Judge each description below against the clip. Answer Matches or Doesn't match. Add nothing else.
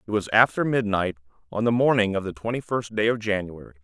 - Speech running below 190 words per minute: Doesn't match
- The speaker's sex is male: Matches